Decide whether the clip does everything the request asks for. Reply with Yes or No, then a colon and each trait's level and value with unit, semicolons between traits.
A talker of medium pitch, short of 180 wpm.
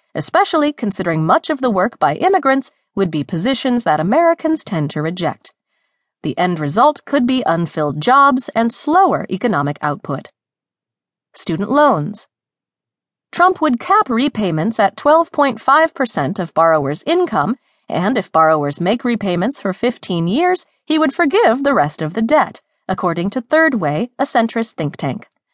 No: high, 235 Hz; average, 145 wpm